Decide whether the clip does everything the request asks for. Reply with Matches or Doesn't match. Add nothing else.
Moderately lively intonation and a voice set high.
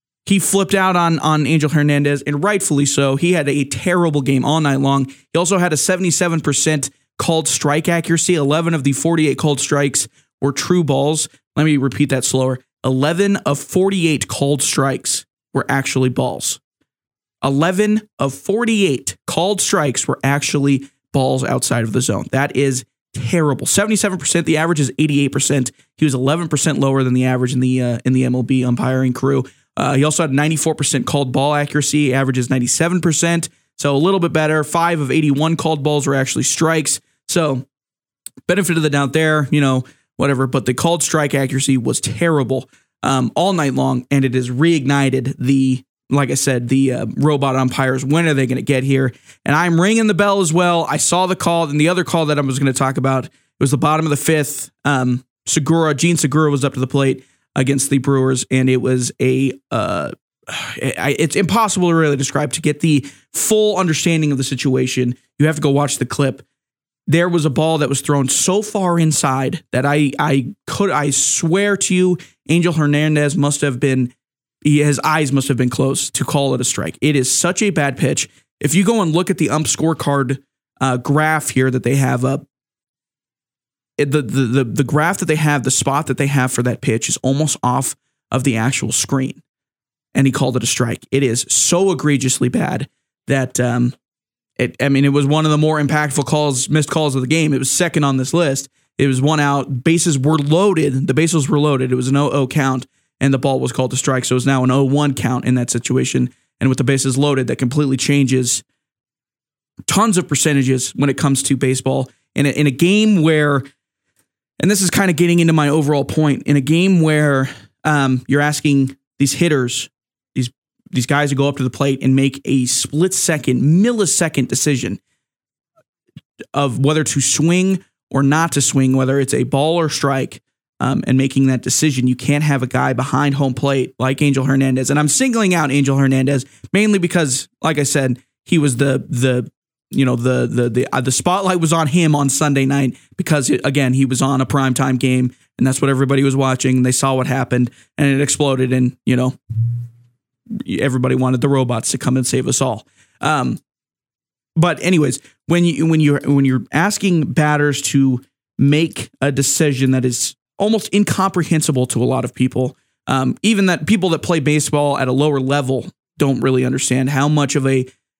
Doesn't match